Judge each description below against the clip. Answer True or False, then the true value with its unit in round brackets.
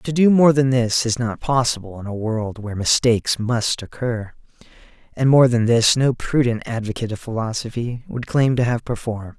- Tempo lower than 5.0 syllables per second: False (5.1 syllables/s)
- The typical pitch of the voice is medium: False (120 Hz)